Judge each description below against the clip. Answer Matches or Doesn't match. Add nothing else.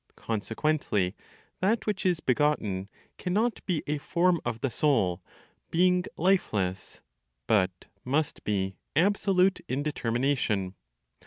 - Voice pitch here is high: Doesn't match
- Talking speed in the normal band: Doesn't match